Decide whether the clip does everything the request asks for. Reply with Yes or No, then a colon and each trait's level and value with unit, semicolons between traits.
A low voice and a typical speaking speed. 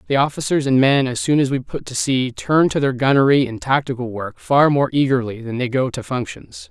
No: low, 130 Hz; fast, 235 wpm